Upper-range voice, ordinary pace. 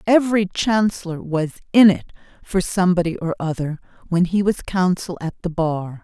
No: medium, 180 Hz; average, 160 wpm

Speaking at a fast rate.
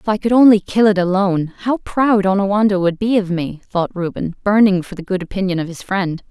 Yes: fast, 230 wpm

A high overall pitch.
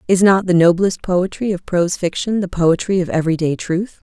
No: medium, 180 Hz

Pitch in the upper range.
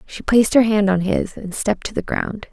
Yes: high, 205 Hz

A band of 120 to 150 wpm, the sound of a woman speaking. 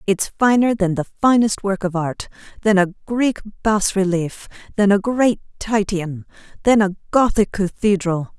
Yes: average, 145 wpm; female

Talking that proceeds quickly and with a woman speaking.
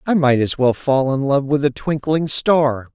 No: fast, 225 wpm; male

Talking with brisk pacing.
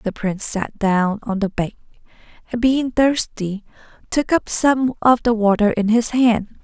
No: average, 170 wpm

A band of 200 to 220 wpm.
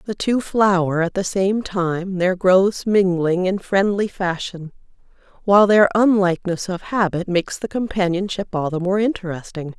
No: average, 155 wpm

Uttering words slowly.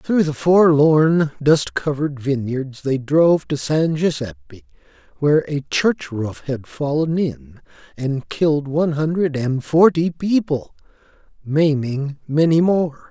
Yes: slow, 130 wpm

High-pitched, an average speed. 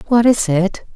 Yes: high, 210 Hz; average, 190 wpm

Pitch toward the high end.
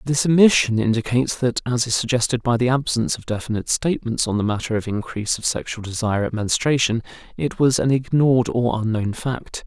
No: low, 120 Hz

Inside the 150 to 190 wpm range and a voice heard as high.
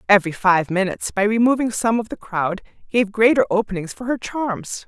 Yes: average, 185 wpm; high, 210 Hz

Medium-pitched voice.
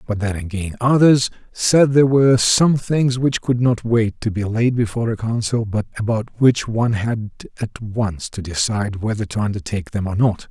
No: low, 110 Hz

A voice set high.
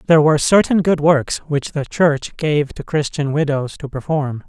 No: medium, 150 Hz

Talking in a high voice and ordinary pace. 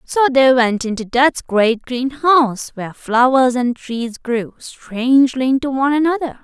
Yes: very high, 255 Hz; average, 150 wpm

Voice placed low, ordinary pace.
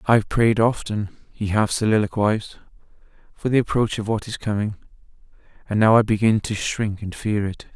Yes: low, 110 Hz; average, 170 wpm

